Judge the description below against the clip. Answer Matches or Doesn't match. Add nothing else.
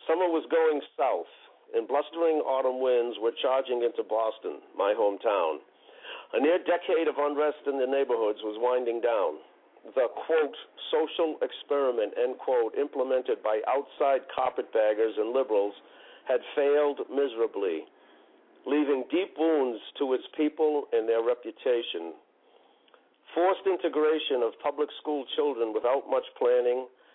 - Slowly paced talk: Matches